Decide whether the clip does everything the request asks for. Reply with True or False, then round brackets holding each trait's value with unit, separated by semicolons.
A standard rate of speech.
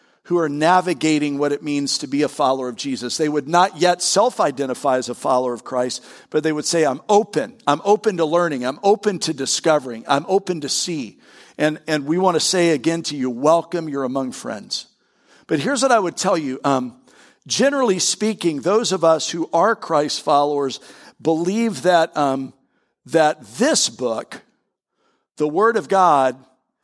True (180 wpm)